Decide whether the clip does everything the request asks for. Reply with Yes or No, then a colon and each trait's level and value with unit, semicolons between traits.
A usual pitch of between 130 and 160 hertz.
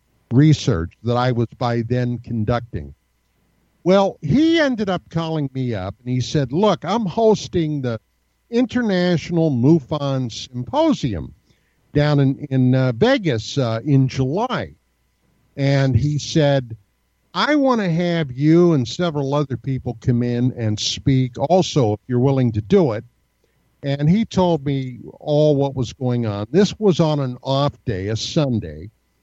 Yes: low, 135 Hz